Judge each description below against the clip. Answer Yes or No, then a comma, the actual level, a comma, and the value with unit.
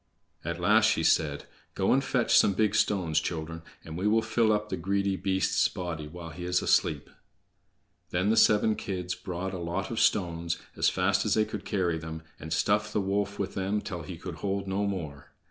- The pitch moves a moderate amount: Yes, average, 3.2 semitones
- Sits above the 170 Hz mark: No, very low, 95 Hz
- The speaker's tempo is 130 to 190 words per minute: No, average, 200 wpm